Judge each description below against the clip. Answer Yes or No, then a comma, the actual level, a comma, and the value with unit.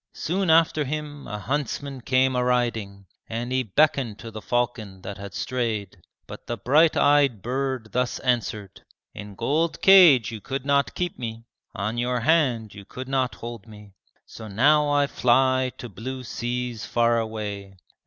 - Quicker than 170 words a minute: No, average, 165 wpm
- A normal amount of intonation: Yes, average, 3.9 semitones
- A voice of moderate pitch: No, low, 125 Hz